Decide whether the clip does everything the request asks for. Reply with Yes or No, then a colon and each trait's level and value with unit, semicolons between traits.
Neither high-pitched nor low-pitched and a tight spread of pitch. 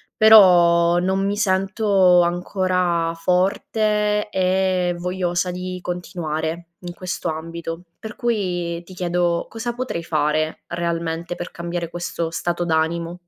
Yes: medium, 175 Hz; narrow, 1.8 semitones